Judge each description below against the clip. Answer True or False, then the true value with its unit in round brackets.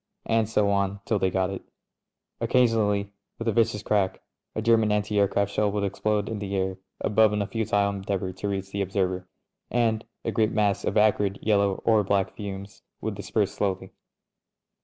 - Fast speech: False (180 wpm)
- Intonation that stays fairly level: True (1.6 semitones)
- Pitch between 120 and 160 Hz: False (100 Hz)